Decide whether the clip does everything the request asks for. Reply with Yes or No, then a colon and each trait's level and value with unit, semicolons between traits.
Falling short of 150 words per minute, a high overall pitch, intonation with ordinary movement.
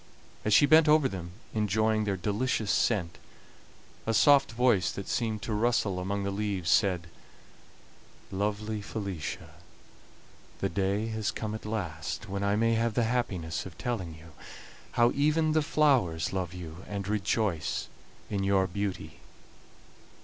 No: average, 140 wpm; low, 105 Hz; average, 3.4 semitones